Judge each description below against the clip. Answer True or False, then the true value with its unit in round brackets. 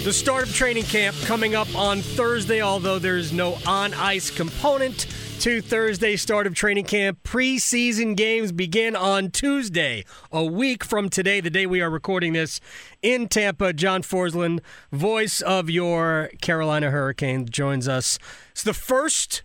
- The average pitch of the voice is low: False (195 Hz)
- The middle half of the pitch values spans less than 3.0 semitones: False (4.7 semitones)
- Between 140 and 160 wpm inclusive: True (155 wpm)